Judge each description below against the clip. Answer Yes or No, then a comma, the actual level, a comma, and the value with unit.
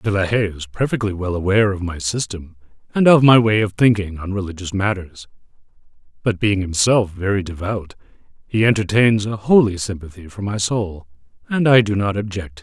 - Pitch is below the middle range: Yes, low, 100 Hz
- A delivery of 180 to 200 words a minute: Yes, average, 185 wpm